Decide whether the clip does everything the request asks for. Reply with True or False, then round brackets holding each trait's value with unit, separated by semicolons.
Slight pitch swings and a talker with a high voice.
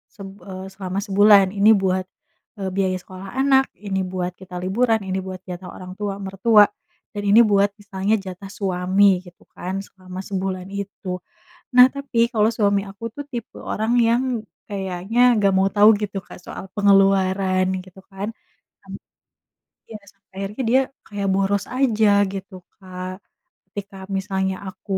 True (1.6 semitones; 195 Hz)